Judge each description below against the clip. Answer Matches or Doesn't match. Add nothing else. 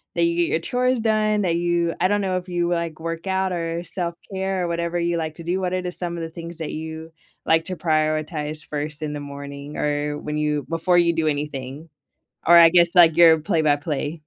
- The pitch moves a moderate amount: Doesn't match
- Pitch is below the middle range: Doesn't match